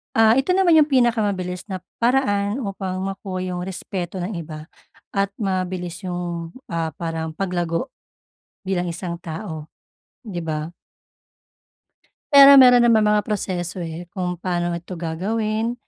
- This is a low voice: No, medium, 185 Hz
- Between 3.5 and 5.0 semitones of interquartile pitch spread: Yes, average, 3.8 semitones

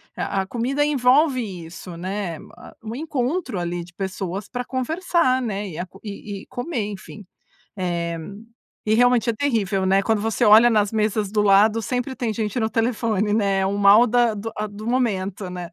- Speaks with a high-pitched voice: Yes, high, 215 Hz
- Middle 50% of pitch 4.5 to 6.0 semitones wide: No, average, 4.0 semitones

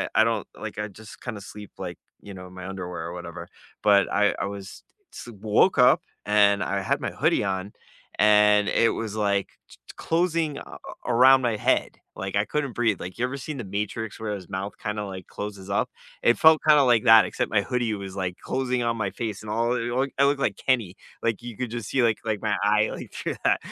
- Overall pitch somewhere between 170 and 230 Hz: No, low, 105 Hz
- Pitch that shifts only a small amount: No, average, 3.2 semitones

